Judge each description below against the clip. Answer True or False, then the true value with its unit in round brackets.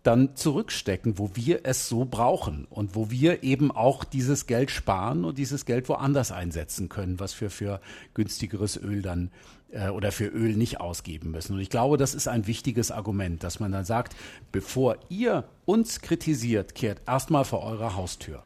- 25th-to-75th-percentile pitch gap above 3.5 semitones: True (5.3 semitones)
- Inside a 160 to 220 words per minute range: True (180 wpm)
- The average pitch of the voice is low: True (115 Hz)